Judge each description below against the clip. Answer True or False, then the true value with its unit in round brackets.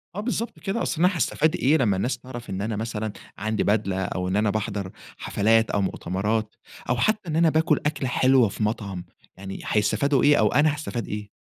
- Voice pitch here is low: True (115 Hz)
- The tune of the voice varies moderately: False (6.5 semitones)